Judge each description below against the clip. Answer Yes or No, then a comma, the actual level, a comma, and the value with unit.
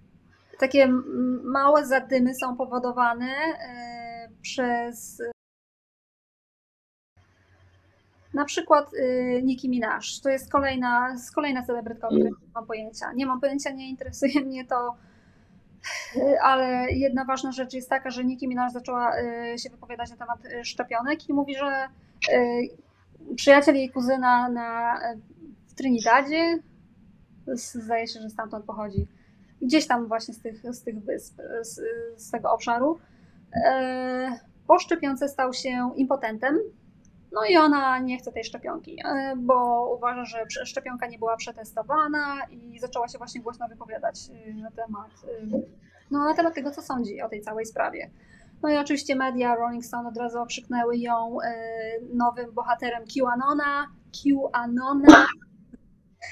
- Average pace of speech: Yes, average, 125 wpm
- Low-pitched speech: No, very high, 250 Hz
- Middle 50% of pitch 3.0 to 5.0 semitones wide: No, narrow, 2.6 semitones